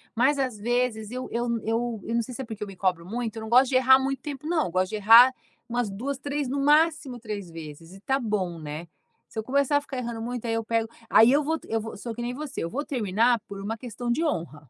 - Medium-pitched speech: No, high, 235 Hz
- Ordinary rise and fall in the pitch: Yes, average, 3.9 semitones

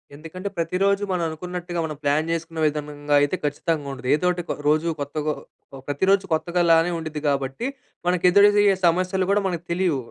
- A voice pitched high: No, medium, 165 Hz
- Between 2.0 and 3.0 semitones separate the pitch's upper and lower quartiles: No, average, 3.4 semitones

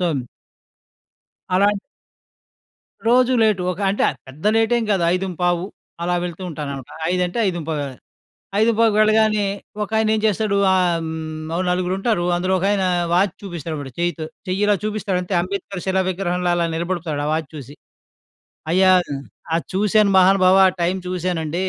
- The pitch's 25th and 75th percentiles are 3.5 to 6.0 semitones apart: No, average, 3.1 semitones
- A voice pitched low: No, medium, 185 Hz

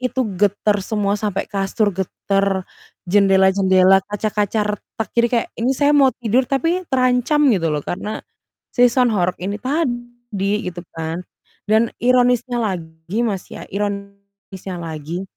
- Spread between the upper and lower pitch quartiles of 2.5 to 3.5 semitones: No, average, 4.1 semitones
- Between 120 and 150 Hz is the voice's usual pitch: No, high, 205 Hz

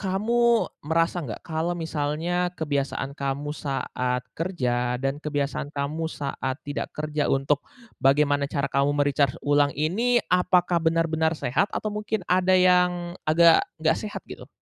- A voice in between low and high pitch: Yes, medium, 155 Hz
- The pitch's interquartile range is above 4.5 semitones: No, average, 3.9 semitones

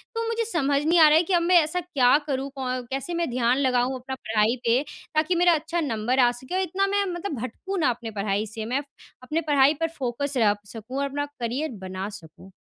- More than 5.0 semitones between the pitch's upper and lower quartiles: Yes, wide, 5.6 semitones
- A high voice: Yes, very high, 270 Hz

